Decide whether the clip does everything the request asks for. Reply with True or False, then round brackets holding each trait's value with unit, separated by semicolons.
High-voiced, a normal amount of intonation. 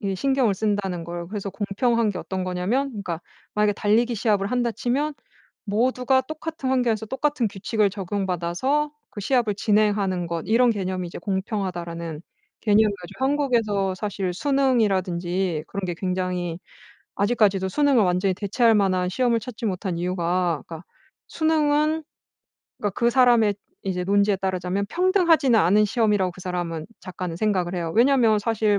True (205 Hz; 4.7 semitones)